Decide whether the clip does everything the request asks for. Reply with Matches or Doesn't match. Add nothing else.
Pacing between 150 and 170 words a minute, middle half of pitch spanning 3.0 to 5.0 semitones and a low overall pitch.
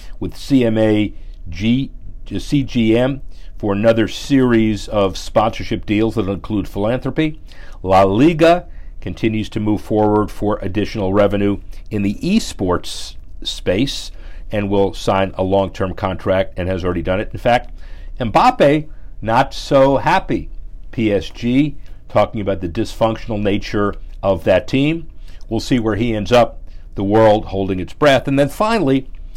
Doesn't match